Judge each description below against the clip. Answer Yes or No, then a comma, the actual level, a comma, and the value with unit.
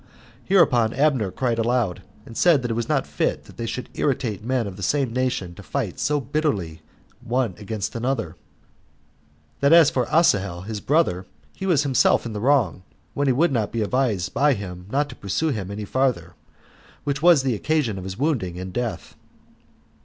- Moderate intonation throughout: No, wide, 5.7 semitones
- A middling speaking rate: Yes, average, 185 wpm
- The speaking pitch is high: No, low, 120 Hz